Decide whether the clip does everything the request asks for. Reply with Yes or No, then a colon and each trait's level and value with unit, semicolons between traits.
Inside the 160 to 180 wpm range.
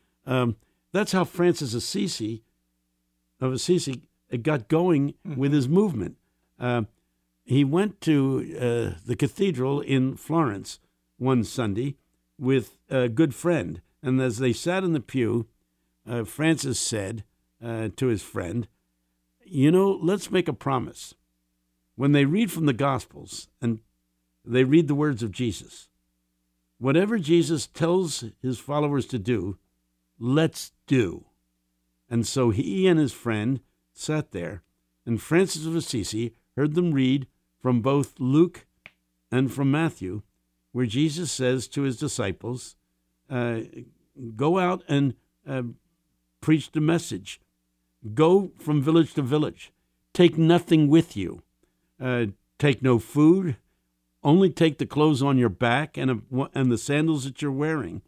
No: slow, 135 wpm